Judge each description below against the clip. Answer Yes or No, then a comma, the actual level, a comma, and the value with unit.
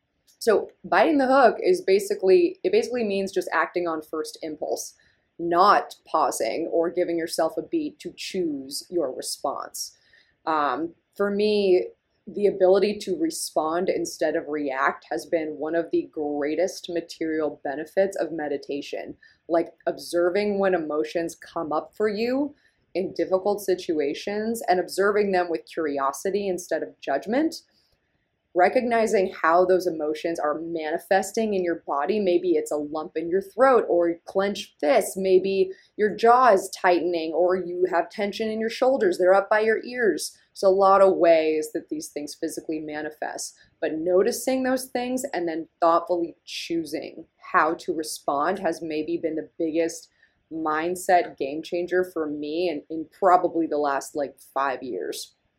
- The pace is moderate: Yes, average, 150 wpm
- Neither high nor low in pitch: Yes, medium, 180 Hz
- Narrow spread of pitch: No, average, 4.3 semitones